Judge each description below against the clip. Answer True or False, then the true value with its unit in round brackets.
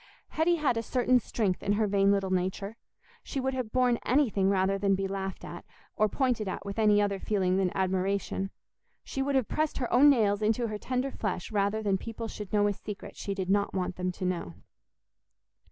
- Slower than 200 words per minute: False (205 wpm)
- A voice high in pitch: True (205 Hz)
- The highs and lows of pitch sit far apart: False (3.7 semitones)